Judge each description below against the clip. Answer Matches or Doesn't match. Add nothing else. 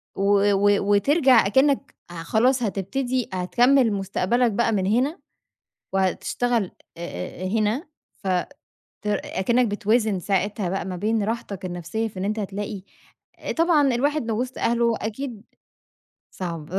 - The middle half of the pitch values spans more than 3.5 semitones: Matches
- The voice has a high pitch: Matches